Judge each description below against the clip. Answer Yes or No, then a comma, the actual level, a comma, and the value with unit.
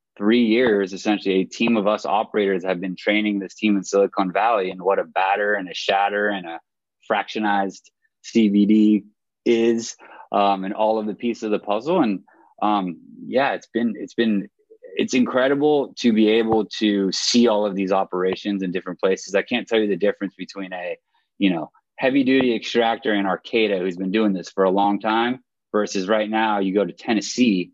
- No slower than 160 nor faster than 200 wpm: Yes, average, 190 wpm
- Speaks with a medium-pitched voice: No, low, 105 Hz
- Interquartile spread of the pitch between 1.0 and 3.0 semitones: Yes, average, 2.7 semitones